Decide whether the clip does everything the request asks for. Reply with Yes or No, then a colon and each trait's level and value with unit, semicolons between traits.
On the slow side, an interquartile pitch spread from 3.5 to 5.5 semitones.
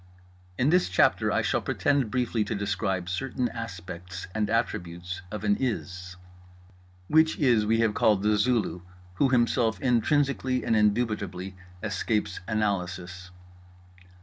Yes: slow, 125 wpm; average, 4.7 semitones